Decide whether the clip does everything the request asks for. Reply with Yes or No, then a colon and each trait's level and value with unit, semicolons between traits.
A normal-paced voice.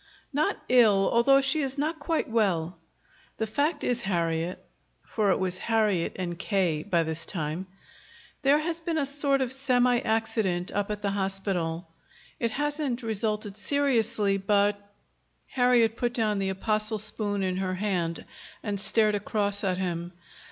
Yes: average, 155 wpm